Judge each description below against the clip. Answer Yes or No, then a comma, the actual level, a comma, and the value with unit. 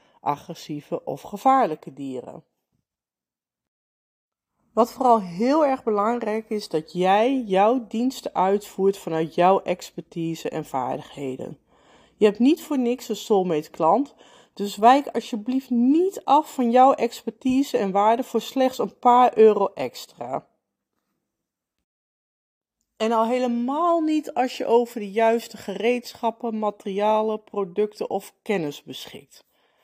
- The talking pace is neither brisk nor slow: No, slow, 120 wpm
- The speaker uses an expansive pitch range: No, average, 4.2 semitones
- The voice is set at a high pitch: Yes, high, 220 Hz